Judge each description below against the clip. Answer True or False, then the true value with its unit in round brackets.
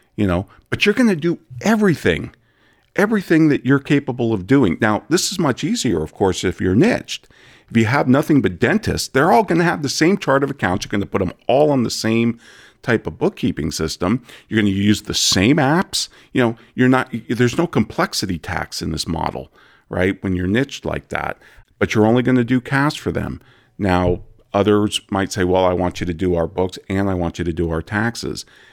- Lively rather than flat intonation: True (6.9 semitones)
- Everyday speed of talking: False (220 wpm)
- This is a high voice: False (110 Hz)